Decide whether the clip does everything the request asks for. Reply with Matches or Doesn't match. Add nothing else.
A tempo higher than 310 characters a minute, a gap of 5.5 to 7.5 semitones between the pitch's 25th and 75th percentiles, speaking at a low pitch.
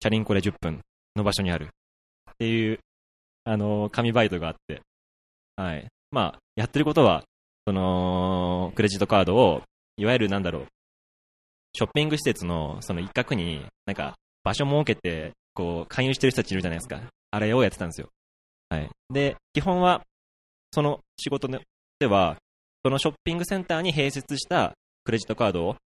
Doesn't match